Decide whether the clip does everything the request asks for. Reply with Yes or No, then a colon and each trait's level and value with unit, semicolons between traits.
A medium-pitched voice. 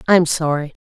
Yes: medium, 160 Hz